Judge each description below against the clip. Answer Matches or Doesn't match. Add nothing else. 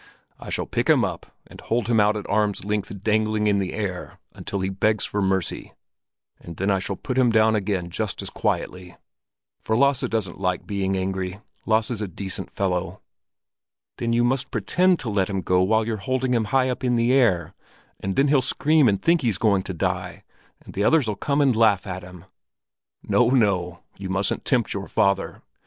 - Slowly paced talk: Doesn't match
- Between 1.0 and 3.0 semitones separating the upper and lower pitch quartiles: Doesn't match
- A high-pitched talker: Doesn't match